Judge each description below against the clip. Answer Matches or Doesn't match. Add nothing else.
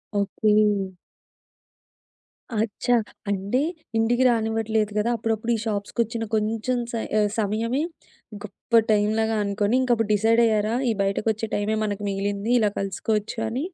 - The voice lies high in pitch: Matches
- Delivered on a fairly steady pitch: Matches